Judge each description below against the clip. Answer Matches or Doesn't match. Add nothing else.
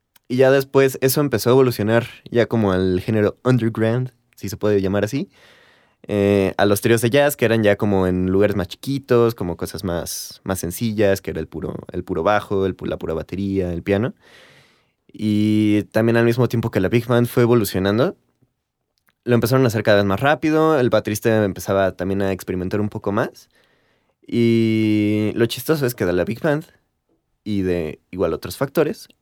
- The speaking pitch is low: Matches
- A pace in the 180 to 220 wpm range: Matches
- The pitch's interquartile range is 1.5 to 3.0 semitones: Doesn't match